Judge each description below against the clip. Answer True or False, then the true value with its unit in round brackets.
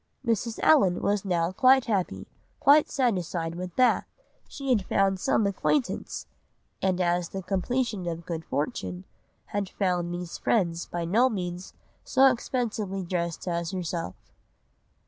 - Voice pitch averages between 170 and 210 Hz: True (185 Hz)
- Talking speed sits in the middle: False (130 wpm)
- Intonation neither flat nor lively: True (4.8 semitones)